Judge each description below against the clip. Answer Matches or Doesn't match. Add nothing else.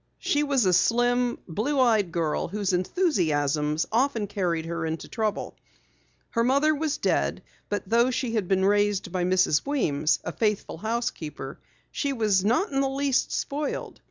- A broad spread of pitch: Matches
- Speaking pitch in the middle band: Doesn't match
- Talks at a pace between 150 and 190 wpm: Matches